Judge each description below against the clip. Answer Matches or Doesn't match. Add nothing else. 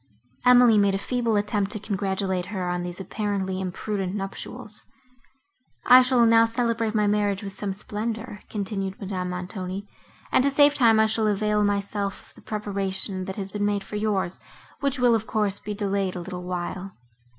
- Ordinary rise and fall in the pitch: Doesn't match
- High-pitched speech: Matches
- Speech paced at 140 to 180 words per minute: Matches